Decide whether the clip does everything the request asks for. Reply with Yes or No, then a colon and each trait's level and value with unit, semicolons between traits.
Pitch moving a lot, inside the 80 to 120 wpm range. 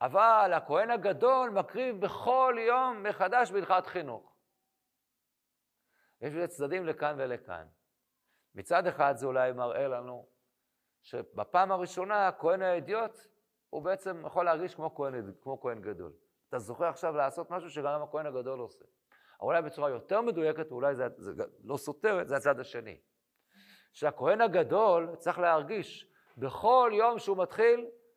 No: wide, 6.7 semitones; average, 130 wpm